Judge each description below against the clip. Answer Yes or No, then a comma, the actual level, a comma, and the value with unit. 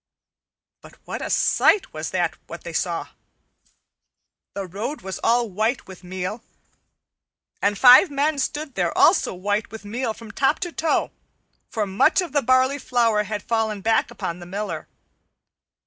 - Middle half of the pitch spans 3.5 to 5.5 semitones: Yes, average, 4.9 semitones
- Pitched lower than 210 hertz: No, high, 225 Hz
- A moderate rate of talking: Yes, average, 155 wpm